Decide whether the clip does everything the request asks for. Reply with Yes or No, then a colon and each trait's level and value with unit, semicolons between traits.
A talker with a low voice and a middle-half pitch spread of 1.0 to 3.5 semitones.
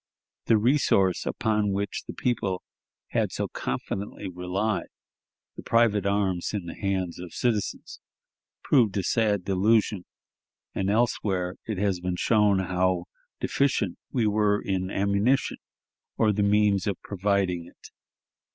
Yes: low, 100 Hz; narrow, 2.5 semitones